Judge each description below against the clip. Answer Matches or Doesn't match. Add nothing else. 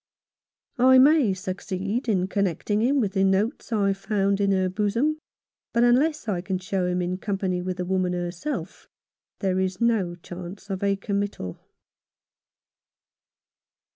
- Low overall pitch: Doesn't match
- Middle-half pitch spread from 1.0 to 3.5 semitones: Matches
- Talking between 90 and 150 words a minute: Matches